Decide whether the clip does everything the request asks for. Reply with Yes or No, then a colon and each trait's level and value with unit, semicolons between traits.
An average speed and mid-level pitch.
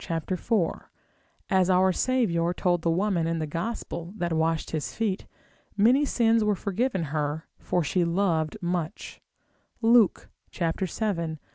No: slow, 130 wpm; medium, 180 Hz